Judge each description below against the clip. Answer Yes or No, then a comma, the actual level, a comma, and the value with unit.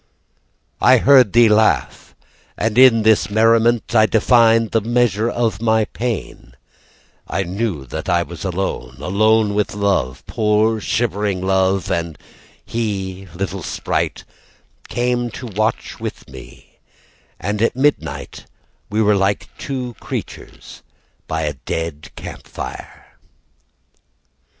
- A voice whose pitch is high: No, low, 105 Hz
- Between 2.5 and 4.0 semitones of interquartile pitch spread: Yes, average, 3.3 semitones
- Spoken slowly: Yes, slow, 120 wpm